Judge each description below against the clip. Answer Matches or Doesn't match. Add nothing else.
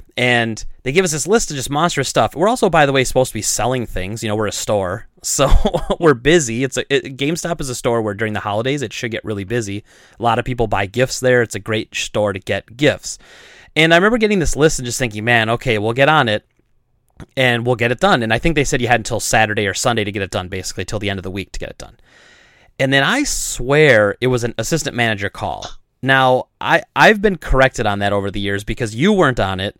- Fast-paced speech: Matches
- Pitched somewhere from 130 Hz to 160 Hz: Doesn't match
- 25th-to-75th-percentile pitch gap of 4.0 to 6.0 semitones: Matches